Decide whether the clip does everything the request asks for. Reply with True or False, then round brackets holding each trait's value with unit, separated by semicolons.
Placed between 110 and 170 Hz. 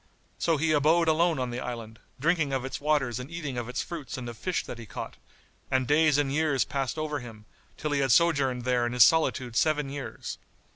True (140 Hz)